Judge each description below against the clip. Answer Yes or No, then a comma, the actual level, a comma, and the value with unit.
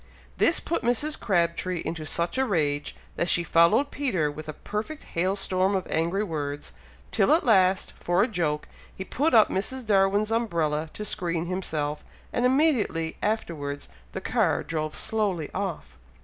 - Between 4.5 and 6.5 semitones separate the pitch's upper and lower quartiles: Yes, average, 5.2 semitones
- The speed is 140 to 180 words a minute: Yes, average, 160 wpm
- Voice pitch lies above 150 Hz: Yes, medium, 185 Hz